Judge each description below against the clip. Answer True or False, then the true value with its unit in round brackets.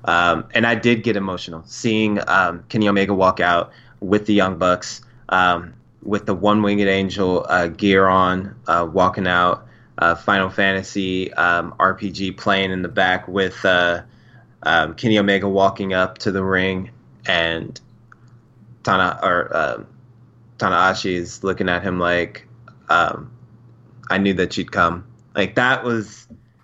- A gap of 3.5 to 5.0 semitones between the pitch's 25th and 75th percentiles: True (3.8 semitones)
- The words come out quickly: False (150 wpm)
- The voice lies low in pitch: True (100 Hz)